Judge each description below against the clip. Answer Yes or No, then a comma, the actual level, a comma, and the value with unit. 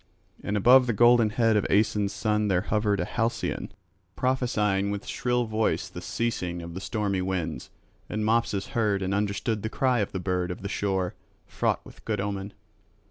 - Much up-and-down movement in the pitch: No, average, 2.7 semitones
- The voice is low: Yes, low, 105 Hz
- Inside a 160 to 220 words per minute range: Yes, average, 180 wpm